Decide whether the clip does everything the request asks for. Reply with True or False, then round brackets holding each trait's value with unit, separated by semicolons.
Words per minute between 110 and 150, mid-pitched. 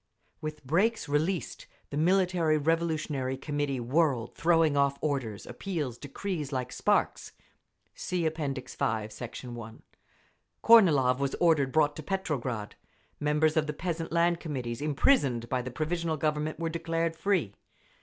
True (135 wpm; 150 Hz)